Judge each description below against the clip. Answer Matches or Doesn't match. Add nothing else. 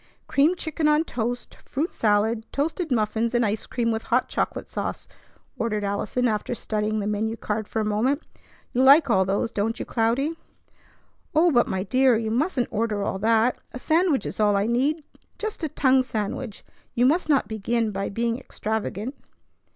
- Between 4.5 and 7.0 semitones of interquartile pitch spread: Doesn't match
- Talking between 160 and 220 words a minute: Matches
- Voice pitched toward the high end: Matches